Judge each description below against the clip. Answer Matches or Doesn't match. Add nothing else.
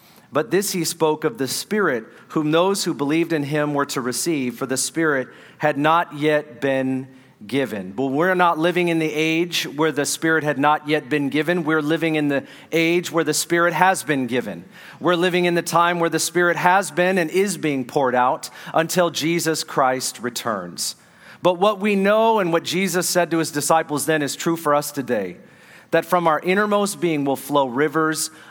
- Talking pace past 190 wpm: Matches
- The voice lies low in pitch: Doesn't match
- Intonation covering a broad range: Doesn't match